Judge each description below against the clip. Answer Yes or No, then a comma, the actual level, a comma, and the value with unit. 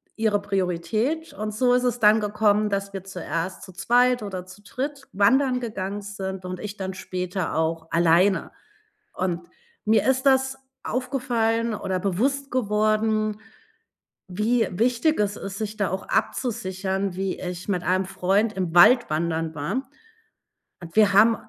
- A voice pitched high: Yes, high, 205 Hz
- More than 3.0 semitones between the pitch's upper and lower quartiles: Yes, average, 3.7 semitones